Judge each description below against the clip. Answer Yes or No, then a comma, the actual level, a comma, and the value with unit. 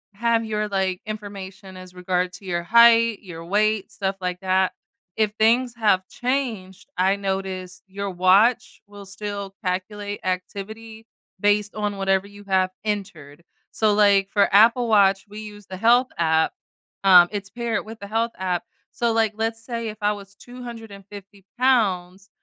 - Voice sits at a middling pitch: No, high, 200 Hz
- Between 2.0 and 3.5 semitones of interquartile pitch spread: Yes, average, 2.7 semitones